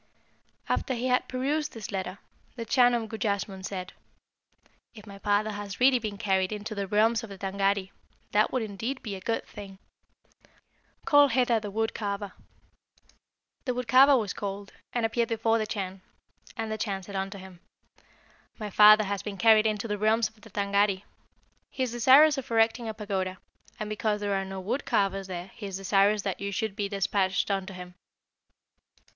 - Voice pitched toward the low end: No, high, 210 Hz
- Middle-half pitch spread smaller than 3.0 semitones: Yes, narrow, 2.5 semitones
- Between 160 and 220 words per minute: Yes, average, 180 wpm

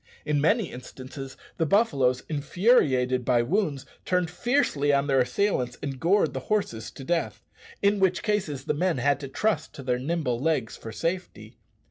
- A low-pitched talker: No, medium, 145 Hz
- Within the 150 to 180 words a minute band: Yes, average, 165 wpm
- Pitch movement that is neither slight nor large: No, wide, 6.2 semitones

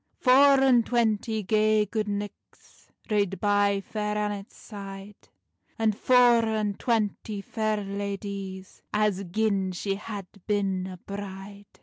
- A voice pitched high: Yes, high, 205 Hz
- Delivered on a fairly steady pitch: Yes, narrow, 1.7 semitones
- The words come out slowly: Yes, slow, 120 wpm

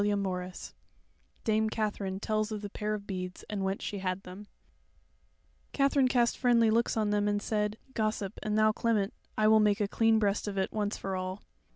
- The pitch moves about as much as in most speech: No, narrow, 1.7 semitones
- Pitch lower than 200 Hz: No, high, 210 Hz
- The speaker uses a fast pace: No, average, 195 wpm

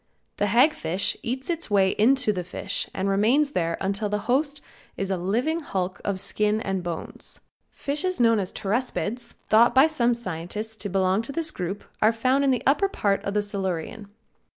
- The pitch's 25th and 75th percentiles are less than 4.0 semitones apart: No, average, 5.0 semitones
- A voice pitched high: Yes, high, 215 Hz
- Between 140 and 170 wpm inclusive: No, average, 185 wpm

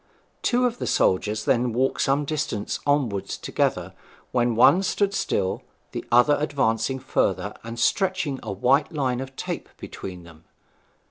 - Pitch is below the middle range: Yes, low, 130 Hz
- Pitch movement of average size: Yes, average, 4.7 semitones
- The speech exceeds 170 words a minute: No, average, 145 wpm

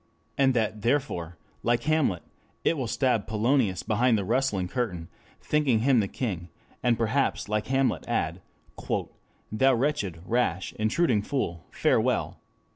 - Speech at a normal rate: No, slow, 130 wpm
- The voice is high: No, low, 115 Hz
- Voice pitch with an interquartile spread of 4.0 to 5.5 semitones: Yes, average, 4.8 semitones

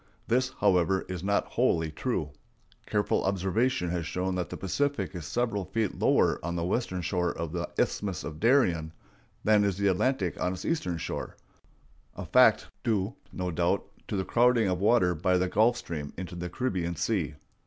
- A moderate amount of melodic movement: Yes, average, 3.6 semitones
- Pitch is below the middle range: Yes, very low, 95 Hz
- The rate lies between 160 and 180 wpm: Yes, average, 175 wpm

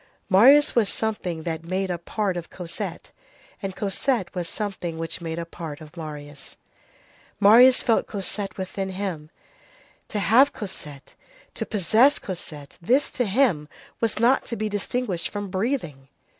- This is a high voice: Yes, high, 195 Hz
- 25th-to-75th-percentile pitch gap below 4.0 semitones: No, average, 4.8 semitones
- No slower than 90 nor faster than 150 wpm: Yes, average, 145 wpm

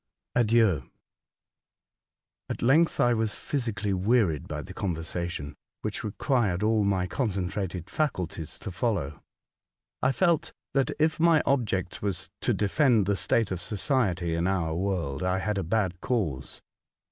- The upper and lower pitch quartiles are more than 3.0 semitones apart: Yes, average, 5.0 semitones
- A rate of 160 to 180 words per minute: No, average, 140 wpm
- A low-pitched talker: Yes, low, 100 Hz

